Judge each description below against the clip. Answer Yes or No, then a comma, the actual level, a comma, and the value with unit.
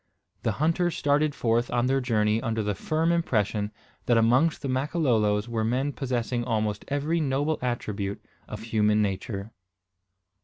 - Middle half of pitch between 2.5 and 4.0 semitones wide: No, average, 5.0 semitones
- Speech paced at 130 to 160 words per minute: Yes, average, 145 wpm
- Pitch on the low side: Yes, low, 120 Hz